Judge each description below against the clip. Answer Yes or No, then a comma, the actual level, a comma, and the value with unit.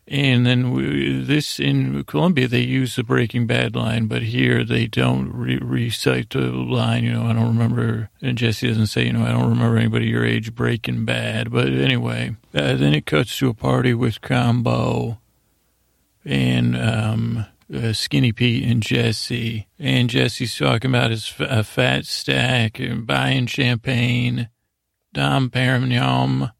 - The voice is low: Yes, low, 115 Hz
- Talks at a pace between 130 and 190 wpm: Yes, average, 160 wpm